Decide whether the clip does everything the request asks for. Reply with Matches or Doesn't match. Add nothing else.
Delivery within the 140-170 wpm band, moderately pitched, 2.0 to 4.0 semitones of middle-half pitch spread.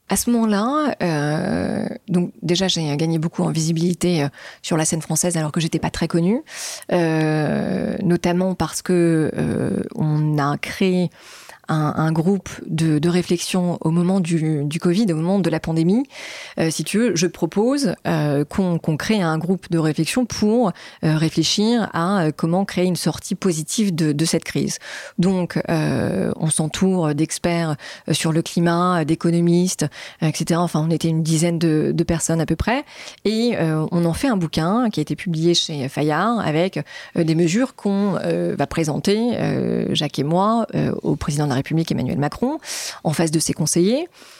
Doesn't match